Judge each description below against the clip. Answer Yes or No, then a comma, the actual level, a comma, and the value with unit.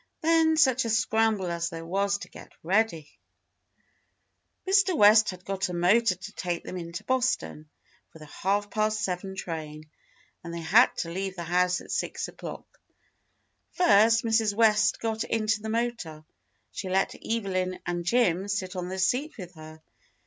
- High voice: Yes, high, 195 Hz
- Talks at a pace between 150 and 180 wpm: Yes, average, 165 wpm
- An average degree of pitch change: Yes, average, 4.2 semitones